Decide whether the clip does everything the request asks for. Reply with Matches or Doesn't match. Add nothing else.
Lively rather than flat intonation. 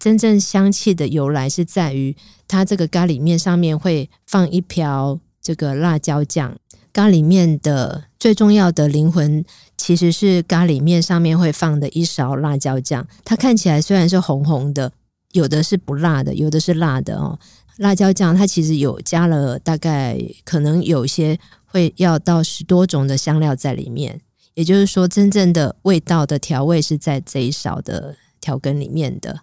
Doesn't match